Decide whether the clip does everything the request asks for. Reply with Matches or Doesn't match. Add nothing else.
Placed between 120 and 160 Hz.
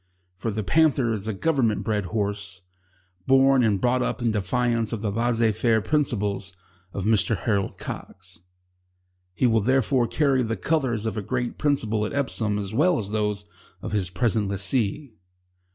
Doesn't match